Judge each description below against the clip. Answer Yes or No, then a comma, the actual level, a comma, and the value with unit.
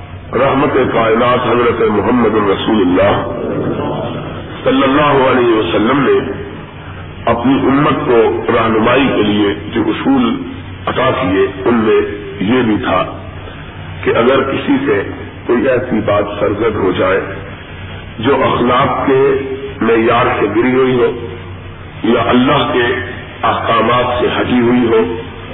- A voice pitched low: Yes, low, 115 Hz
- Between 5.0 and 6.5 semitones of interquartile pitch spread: Yes, wide, 5.4 semitones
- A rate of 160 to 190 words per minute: No, average, 120 wpm